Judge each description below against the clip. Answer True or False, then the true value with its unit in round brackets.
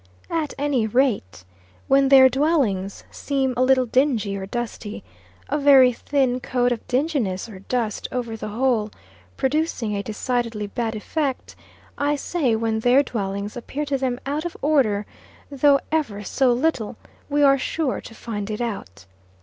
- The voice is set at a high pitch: True (250 Hz)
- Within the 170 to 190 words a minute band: False (155 wpm)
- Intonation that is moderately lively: True (4.2 semitones)